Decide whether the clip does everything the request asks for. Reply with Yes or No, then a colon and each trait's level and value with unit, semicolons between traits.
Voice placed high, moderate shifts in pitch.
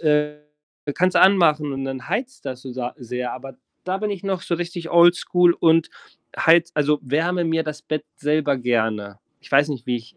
No: medium, 150 Hz; average, 4.7 semitones